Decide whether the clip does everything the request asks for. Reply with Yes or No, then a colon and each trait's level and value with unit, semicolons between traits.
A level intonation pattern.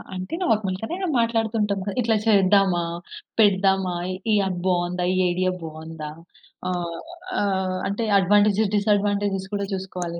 Yes: narrow, 2.3 semitones